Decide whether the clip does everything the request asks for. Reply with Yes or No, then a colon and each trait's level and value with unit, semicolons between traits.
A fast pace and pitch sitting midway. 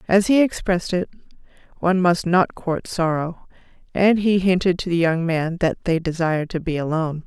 No: average, 180 wpm; medium, 175 Hz